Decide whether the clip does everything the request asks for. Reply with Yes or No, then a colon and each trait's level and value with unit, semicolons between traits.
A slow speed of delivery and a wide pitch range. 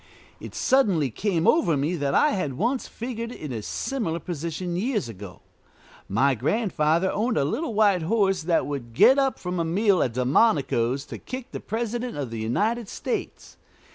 No: average, 170 wpm; wide, 8.4 semitones